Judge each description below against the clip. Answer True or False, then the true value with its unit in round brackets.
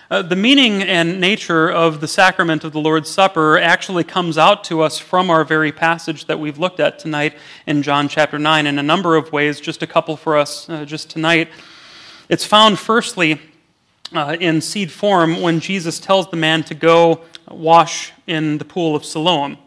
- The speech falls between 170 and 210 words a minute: True (190 wpm)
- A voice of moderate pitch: True (165 Hz)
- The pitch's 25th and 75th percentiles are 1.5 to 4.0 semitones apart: True (2.5 semitones)